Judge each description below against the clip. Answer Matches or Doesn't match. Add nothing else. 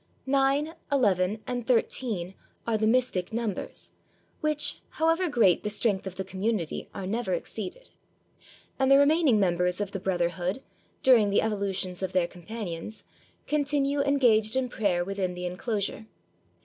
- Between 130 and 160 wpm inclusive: Matches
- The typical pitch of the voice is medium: Doesn't match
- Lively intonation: Matches